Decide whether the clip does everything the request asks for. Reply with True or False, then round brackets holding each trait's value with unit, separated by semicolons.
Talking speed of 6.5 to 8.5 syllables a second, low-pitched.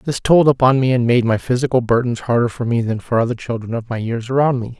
False (6.1 syllables/s; 120 Hz)